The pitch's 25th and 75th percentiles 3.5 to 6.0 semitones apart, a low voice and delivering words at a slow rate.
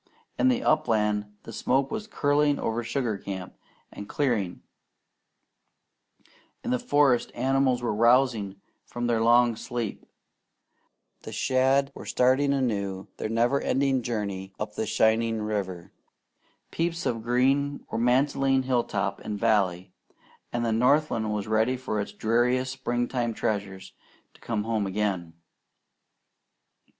Yes: average, 3.8 semitones; low, 120 Hz; slow, 125 wpm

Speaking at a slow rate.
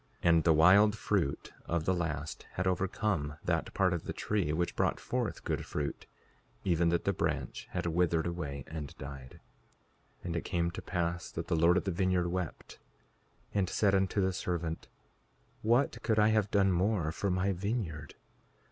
No: average, 180 wpm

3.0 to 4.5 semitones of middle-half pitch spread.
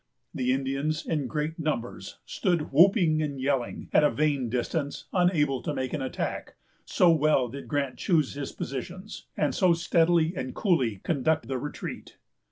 Yes: average, 3.6 semitones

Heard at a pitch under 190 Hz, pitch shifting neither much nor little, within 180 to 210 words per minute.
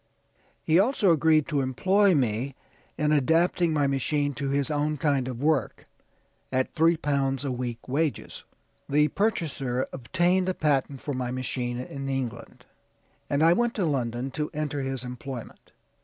No: medium, 140 Hz; average, 3.5 semitones; average, 155 wpm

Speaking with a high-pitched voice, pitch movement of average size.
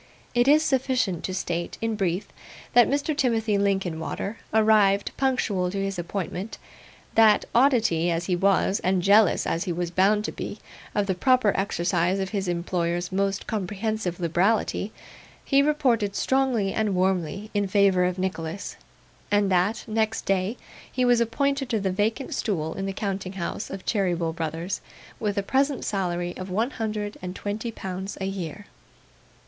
Yes: high, 200 Hz; average, 3.4 semitones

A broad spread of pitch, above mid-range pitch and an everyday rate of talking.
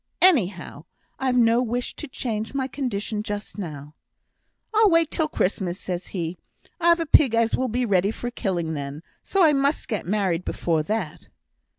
Yes: wide, 6.8 semitones; high, 220 Hz; average, 170 wpm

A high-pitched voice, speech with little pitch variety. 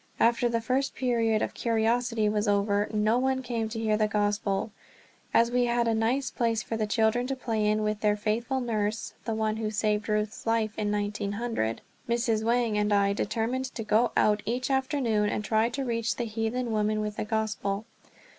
Yes: high, 220 Hz; narrow, 2.0 semitones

